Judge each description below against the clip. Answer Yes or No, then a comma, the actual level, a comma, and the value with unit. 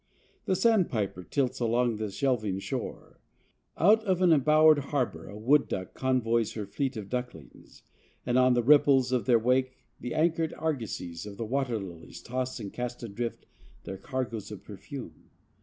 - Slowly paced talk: No, average, 160 wpm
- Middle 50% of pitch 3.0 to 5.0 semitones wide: Yes, average, 4.2 semitones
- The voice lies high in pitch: No, low, 125 Hz